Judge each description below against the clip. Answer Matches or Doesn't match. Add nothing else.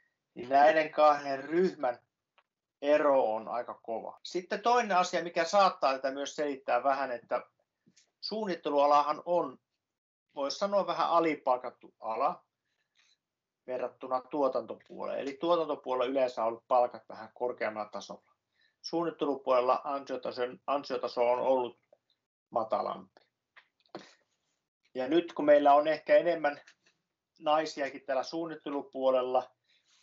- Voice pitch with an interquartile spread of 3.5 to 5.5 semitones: Matches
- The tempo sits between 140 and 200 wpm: Doesn't match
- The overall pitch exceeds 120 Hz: Matches